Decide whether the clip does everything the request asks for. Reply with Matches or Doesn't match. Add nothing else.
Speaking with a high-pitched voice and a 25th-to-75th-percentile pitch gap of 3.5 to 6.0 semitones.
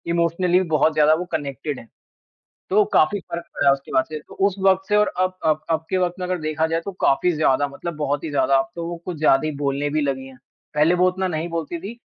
Doesn't match